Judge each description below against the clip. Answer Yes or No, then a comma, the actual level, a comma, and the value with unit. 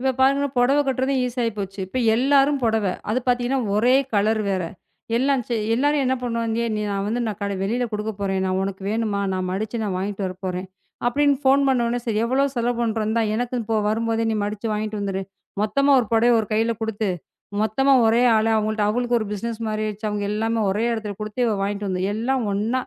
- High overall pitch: Yes, high, 225 Hz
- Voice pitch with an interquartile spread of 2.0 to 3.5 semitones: Yes, average, 2.9 semitones